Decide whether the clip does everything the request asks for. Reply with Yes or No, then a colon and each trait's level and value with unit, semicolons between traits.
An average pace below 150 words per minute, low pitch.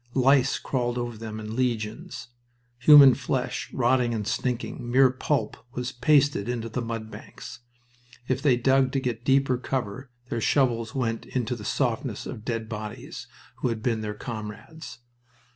No: average, 155 wpm; low, 120 Hz